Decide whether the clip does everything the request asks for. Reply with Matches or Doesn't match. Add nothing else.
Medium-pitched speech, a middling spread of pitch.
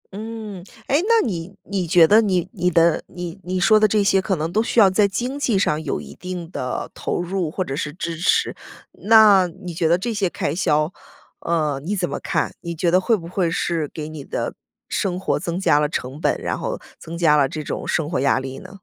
Matches